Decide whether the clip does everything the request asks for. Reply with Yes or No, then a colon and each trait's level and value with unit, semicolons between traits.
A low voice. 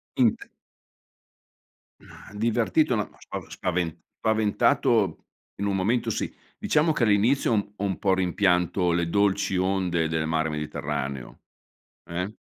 Yes: very low, 95 Hz